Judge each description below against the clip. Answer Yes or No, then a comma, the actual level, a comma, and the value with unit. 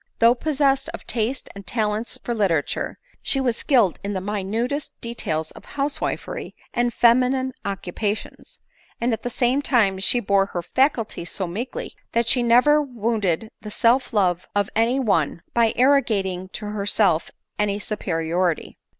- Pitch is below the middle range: No, high, 225 Hz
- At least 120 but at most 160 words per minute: Yes, average, 150 wpm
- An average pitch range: Yes, average, 4.3 semitones